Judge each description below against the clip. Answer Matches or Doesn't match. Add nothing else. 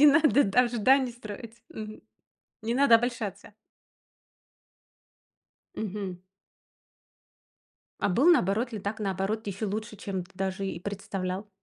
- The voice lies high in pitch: Matches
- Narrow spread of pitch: Doesn't match